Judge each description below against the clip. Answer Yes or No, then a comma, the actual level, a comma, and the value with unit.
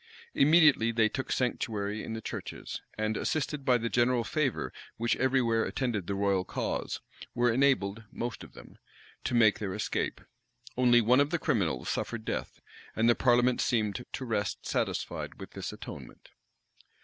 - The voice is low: Yes, low, 120 Hz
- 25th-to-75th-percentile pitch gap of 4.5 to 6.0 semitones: No, average, 2.9 semitones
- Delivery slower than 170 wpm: Yes, average, 160 wpm